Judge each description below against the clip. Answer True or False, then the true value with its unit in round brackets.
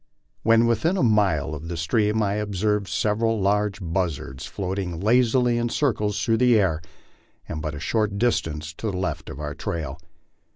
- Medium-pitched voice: False (100 Hz)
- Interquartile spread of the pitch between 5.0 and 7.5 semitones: True (5.3 semitones)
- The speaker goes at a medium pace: True (175 wpm)